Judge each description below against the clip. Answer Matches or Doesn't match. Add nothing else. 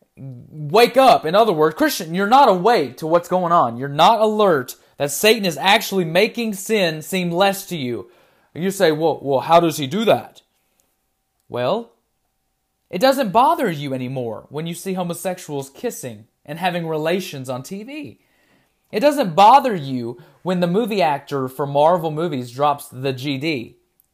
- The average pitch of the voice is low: Doesn't match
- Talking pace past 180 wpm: Doesn't match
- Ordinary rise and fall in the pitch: Doesn't match